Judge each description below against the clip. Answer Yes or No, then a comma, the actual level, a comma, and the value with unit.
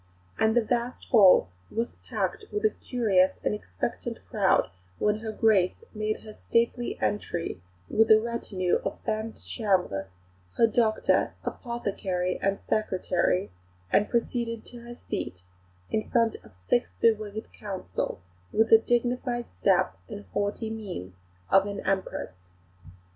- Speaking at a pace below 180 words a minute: Yes, slow, 135 wpm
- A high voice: Yes, high, 215 Hz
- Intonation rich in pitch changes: No, average, 3.6 semitones